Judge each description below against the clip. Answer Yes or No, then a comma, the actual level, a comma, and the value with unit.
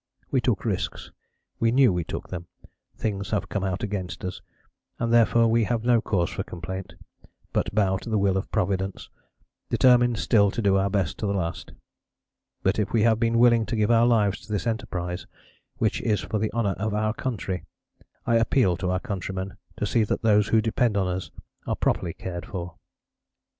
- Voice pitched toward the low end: Yes, low, 105 Hz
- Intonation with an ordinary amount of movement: Yes, average, 3.4 semitones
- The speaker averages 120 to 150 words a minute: No, average, 195 wpm